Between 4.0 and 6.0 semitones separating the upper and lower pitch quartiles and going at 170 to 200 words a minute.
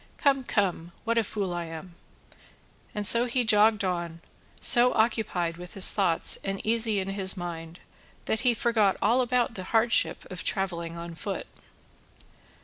No: average, 4.7 semitones; average, 155 wpm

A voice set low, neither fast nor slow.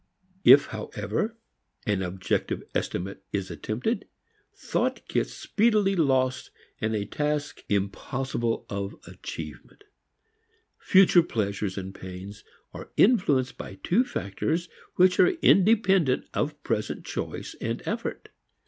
No: low, 130 Hz; slow, 110 wpm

